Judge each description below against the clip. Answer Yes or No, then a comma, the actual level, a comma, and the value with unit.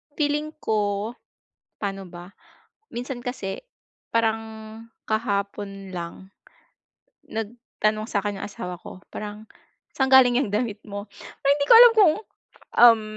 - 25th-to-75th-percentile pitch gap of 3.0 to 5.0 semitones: Yes, average, 3.7 semitones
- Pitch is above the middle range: Yes, high, 215 Hz